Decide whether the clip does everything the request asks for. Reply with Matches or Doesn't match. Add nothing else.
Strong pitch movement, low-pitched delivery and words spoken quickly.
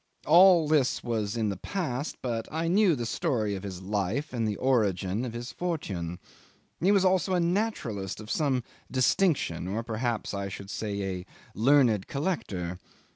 Doesn't match